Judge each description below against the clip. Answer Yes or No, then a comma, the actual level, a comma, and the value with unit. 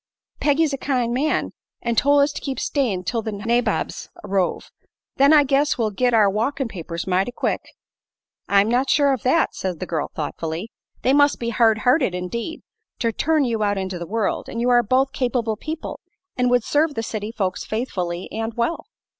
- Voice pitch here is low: No, high, 235 Hz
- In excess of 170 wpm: Yes, average, 190 wpm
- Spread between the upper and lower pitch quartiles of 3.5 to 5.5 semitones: Yes, average, 5.1 semitones